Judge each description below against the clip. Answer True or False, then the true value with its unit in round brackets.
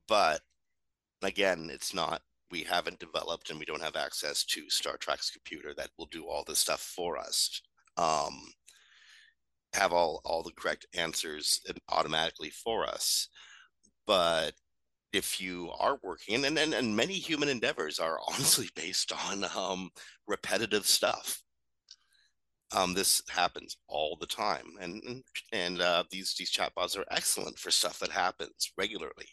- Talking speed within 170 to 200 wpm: False (145 wpm)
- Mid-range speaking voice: False (105 Hz)